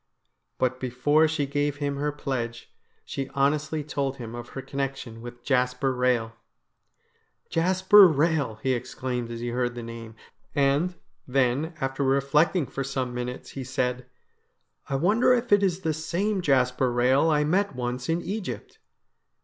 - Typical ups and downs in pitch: Yes, average, 3.8 semitones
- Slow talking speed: No, average, 160 wpm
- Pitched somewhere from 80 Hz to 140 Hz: Yes, low, 135 Hz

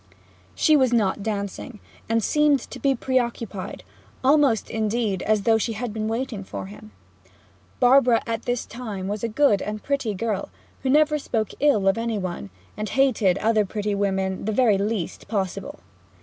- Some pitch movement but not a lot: Yes, average, 3.6 semitones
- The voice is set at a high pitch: Yes, high, 220 Hz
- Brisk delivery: No, average, 165 wpm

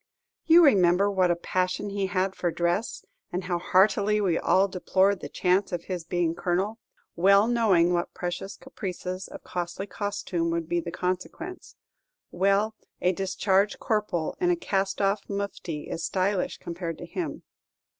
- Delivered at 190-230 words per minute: No, average, 155 wpm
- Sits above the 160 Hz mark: Yes, high, 190 Hz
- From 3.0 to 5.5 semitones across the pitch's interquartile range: No, narrow, 2.4 semitones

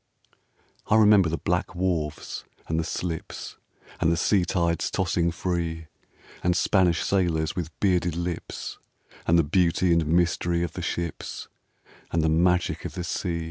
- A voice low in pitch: Yes, very low, 85 Hz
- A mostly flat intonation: Yes, narrow, 1.5 semitones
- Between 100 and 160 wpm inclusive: Yes, average, 150 wpm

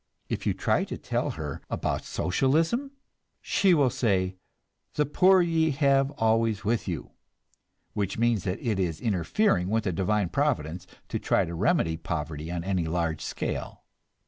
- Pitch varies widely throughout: Yes, wide, 8.0 semitones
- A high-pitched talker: No, low, 100 Hz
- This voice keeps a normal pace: Yes, average, 150 wpm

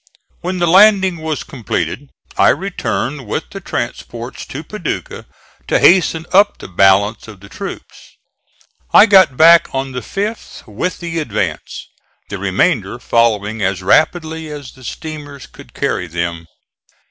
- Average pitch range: No, wide, 8.2 semitones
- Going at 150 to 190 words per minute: No, average, 140 wpm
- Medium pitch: Yes, medium, 145 Hz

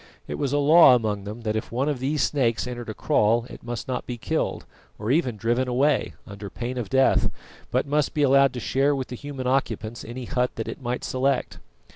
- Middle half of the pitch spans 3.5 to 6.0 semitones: No, average, 2.8 semitones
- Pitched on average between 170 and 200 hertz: No, low, 125 Hz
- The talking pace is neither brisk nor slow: No, fast, 220 wpm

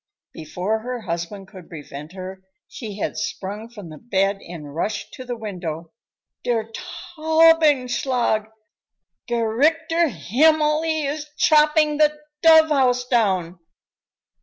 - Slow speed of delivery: Yes, slow, 115 wpm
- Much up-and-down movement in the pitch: Yes, wide, 8.1 semitones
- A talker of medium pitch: No, high, 235 Hz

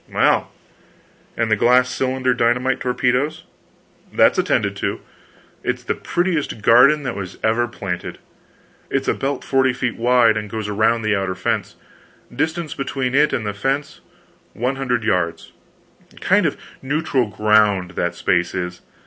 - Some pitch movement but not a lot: Yes, average, 4.1 semitones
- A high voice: No, low, 120 Hz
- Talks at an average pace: Yes, average, 145 wpm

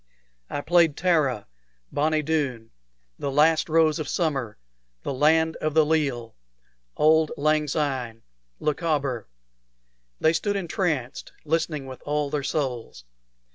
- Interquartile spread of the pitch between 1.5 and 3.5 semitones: Yes, average, 2.9 semitones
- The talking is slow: Yes, slow, 120 wpm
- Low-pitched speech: No, medium, 150 Hz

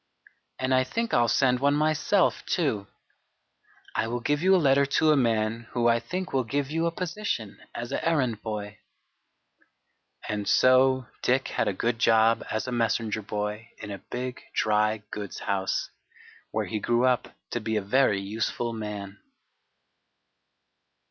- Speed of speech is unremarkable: Yes, average, 160 wpm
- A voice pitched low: Yes, low, 120 Hz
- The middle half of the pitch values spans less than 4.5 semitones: Yes, average, 4.1 semitones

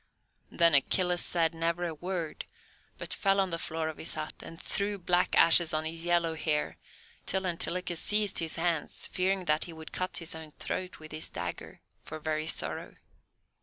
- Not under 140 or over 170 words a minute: No, average, 180 wpm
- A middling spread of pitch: No, narrow, 2.2 semitones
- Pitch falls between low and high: Yes, medium, 165 Hz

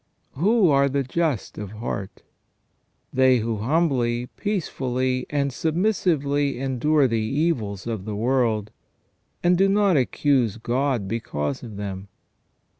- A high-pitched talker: No, low, 130 Hz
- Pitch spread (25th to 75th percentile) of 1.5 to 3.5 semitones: No, average, 4.9 semitones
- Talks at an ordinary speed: No, slow, 120 wpm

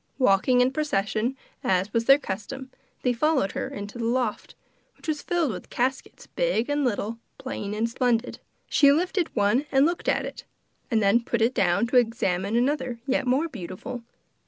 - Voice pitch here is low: No, high, 245 Hz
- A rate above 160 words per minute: Yes, average, 180 wpm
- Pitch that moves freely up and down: No, average, 4.3 semitones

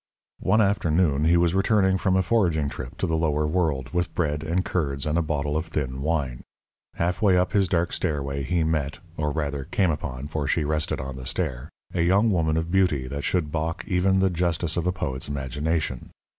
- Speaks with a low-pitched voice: Yes, very low, 80 Hz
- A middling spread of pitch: Yes, average, 3.7 semitones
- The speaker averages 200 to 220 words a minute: Yes, fast, 205 wpm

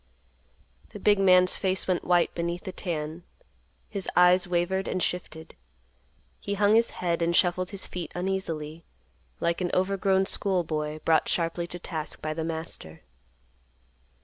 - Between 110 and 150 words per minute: Yes, average, 145 wpm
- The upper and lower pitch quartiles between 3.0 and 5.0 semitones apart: No, narrow, 2.4 semitones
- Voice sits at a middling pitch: Yes, medium, 175 Hz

